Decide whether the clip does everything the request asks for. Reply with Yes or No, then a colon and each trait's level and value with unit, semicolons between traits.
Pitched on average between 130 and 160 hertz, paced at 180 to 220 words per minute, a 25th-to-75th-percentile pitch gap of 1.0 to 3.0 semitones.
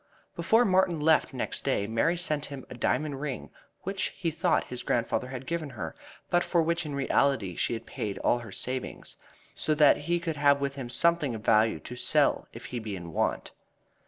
No: medium, 140 Hz; average, 200 wpm; wide, 5.4 semitones